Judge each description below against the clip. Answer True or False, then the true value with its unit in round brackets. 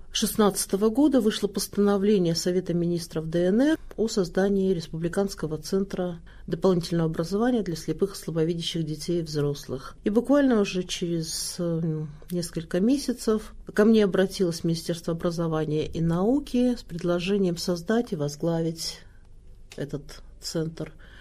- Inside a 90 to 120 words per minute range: True (115 wpm)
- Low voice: False (175 Hz)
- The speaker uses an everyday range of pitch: True (3.5 semitones)